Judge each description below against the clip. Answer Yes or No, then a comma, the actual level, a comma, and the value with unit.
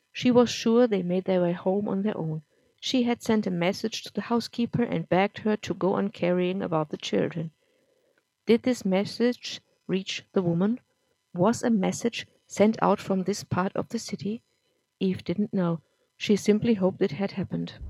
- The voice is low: No, high, 195 Hz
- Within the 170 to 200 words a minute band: Yes, average, 185 wpm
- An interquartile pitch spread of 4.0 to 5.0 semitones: No, average, 3.6 semitones